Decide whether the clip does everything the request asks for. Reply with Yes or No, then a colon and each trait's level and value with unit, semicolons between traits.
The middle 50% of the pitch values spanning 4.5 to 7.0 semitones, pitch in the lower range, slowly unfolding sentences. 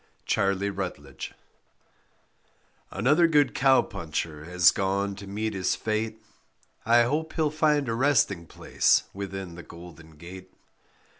Yes: wide, 5.6 semitones; low, 100 Hz; slow, 125 wpm